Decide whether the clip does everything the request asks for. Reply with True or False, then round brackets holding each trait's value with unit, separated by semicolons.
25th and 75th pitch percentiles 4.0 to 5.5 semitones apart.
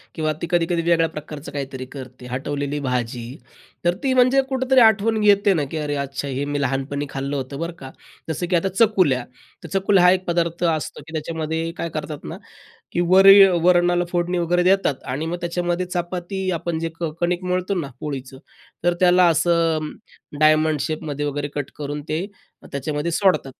False (3.6 semitones)